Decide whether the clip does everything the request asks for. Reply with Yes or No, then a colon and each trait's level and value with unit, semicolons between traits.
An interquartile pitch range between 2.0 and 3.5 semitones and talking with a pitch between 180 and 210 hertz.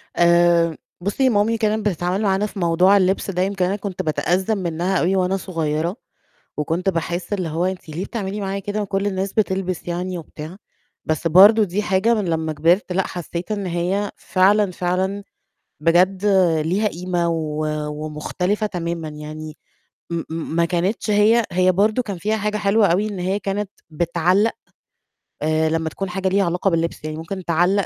Yes: average, 3.0 semitones; medium, 185 Hz